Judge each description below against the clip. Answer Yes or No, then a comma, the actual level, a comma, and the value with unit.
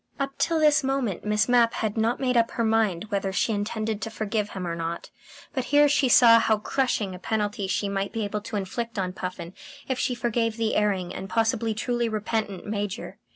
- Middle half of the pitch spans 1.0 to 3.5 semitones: Yes, average, 2.9 semitones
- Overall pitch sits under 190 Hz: No, high, 220 Hz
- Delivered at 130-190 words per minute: No, fast, 205 wpm